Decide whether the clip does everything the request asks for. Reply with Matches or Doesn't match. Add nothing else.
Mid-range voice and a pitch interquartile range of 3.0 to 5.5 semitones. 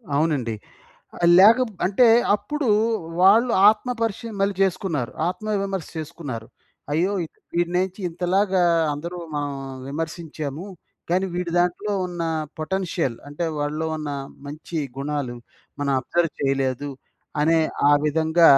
Matches